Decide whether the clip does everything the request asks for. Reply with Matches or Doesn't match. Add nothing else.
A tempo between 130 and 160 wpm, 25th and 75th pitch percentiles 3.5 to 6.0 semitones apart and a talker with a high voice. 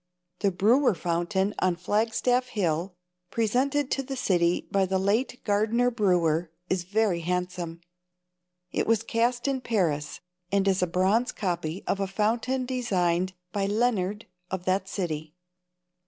Matches